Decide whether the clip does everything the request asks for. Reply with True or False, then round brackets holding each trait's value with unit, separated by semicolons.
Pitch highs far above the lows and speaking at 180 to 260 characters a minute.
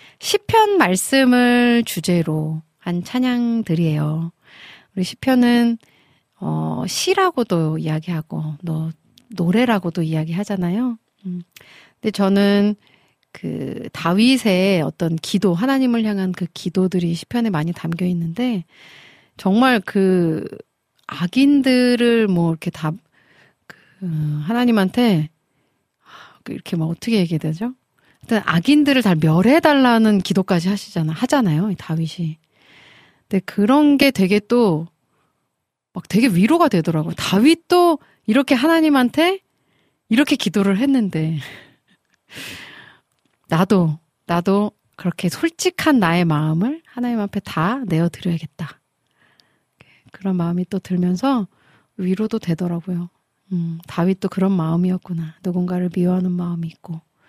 True (6.1 semitones; 255 characters per minute)